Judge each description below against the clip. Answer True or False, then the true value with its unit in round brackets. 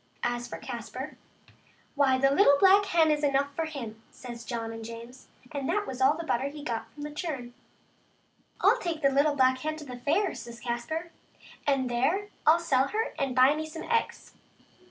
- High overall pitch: True (275 Hz)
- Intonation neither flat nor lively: True (4.2 semitones)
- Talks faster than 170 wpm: True (200 wpm)